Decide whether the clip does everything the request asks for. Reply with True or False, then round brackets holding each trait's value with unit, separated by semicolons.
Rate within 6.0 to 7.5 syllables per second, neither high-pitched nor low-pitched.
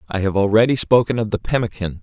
False (6.6 syllables/s; 105 Hz)